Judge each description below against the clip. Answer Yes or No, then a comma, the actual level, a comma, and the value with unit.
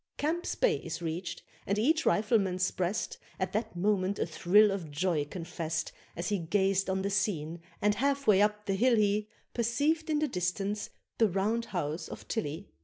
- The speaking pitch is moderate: No, high, 200 Hz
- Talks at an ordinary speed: Yes, average, 180 wpm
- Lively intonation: No, average, 3.7 semitones